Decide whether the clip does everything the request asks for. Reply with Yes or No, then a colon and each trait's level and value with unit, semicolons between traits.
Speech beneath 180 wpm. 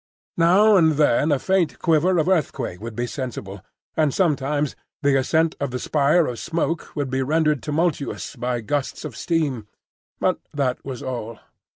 Yes: average, 165 wpm